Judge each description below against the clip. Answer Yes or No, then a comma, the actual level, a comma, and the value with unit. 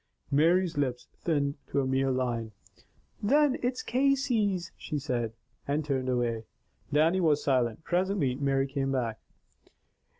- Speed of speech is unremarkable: No, slow, 130 wpm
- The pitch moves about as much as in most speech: No, wide, 5.8 semitones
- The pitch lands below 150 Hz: Yes, medium, 140 Hz